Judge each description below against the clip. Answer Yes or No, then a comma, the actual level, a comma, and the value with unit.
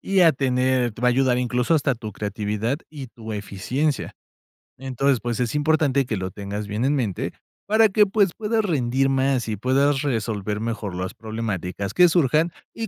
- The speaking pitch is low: Yes, low, 125 Hz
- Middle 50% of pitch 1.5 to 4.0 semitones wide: No, average, 5.1 semitones